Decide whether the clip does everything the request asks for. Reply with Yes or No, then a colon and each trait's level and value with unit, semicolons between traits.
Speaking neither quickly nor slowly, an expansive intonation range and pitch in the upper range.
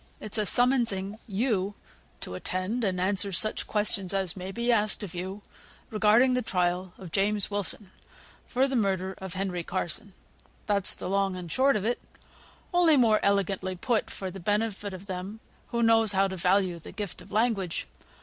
No: average, 175 wpm; average, 2.7 semitones; high, 200 Hz